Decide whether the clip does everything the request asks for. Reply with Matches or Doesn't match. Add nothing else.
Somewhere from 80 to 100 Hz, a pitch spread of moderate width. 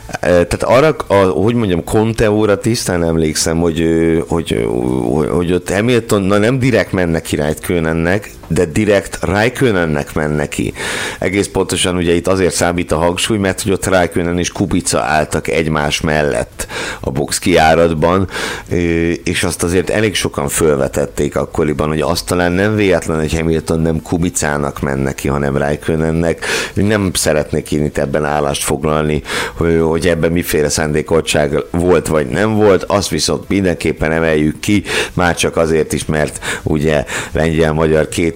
Matches